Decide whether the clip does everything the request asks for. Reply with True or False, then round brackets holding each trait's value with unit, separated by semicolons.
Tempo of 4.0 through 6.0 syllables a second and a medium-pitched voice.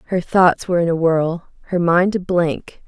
True (4.6 syllables/s; 175 Hz)